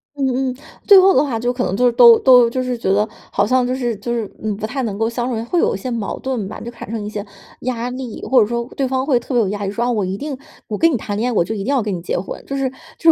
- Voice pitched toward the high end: Yes, high, 240 Hz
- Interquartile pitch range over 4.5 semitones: No, average, 3.2 semitones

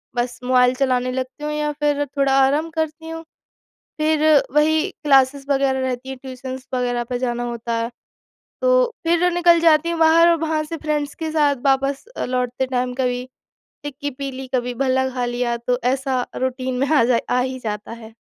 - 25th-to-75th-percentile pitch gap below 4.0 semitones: Yes, average, 3.2 semitones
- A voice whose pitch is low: No, very high, 265 Hz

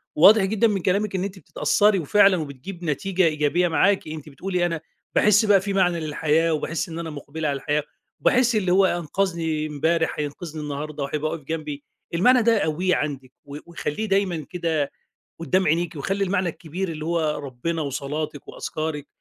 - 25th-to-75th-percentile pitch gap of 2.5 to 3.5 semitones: No, average, 4.0 semitones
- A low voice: No, medium, 165 Hz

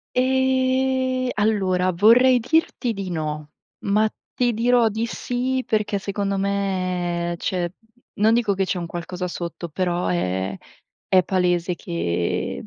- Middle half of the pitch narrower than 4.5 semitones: No, wide, 5.4 semitones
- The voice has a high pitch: Yes, high, 195 Hz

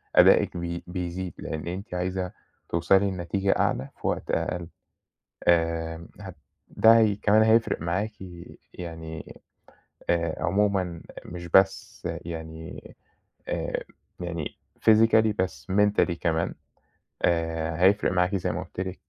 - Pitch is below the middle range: Yes, very low, 90 Hz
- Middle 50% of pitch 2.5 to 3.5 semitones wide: Yes, average, 2.8 semitones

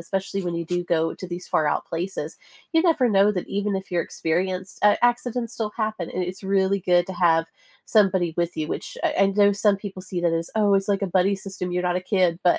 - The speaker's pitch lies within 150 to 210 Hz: Yes, high, 190 Hz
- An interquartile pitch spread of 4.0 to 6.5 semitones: No, narrow, 2.4 semitones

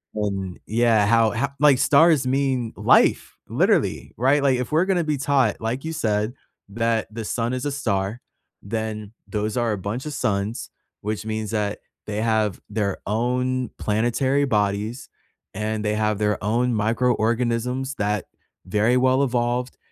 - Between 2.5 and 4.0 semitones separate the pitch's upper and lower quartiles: Yes, average, 3.4 semitones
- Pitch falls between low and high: No, low, 115 Hz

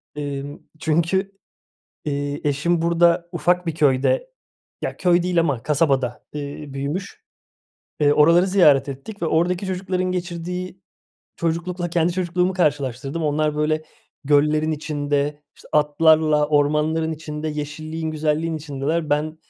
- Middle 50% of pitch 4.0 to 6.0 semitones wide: No, average, 2.8 semitones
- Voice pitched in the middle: Yes, medium, 155 Hz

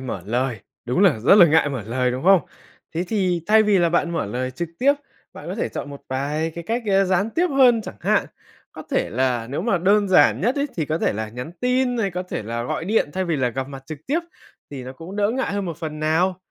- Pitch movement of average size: No, wide, 7.4 semitones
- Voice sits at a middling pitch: Yes, medium, 170 Hz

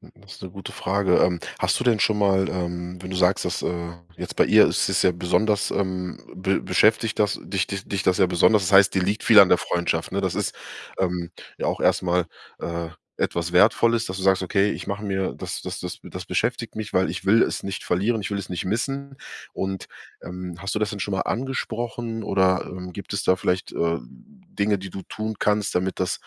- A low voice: Yes, very low, 95 Hz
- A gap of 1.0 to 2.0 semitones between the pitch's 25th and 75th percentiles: No, average, 2.7 semitones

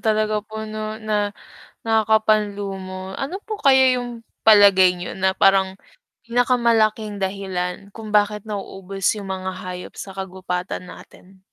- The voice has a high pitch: Yes, high, 205 Hz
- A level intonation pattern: Yes, narrow, 2.3 semitones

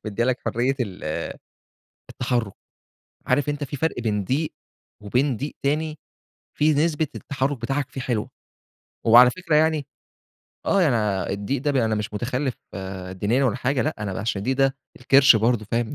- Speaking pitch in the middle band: No, low, 125 Hz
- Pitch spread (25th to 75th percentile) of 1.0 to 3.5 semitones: No, average, 4.3 semitones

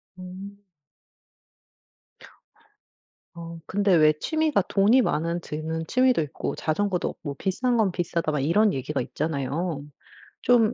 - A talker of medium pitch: Yes, medium, 175 Hz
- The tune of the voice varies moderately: Yes, average, 4.8 semitones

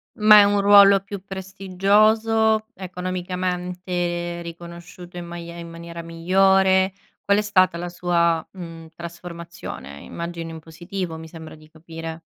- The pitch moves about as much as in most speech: No, narrow, 2.3 semitones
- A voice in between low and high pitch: Yes, medium, 175 Hz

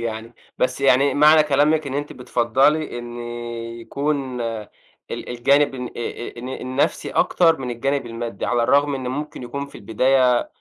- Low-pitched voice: Yes, low, 130 Hz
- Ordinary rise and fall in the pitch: Yes, average, 3.0 semitones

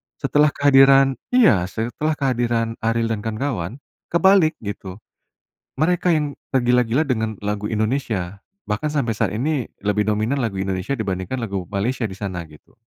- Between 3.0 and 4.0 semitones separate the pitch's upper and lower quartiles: No, average, 5.1 semitones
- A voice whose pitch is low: Yes, low, 115 Hz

